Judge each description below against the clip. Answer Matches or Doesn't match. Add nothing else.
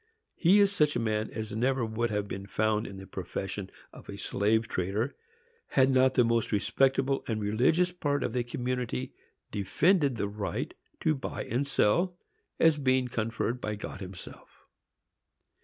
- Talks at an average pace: Matches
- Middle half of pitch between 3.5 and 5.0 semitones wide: Matches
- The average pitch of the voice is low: Matches